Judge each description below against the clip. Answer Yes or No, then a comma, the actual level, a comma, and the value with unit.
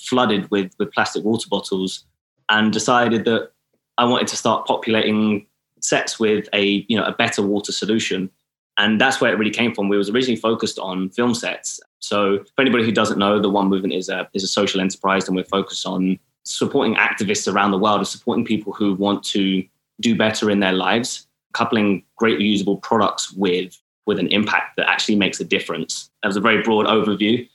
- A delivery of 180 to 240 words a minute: Yes, average, 200 wpm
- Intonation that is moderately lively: No, narrow, 2.3 semitones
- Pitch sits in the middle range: No, low, 105 Hz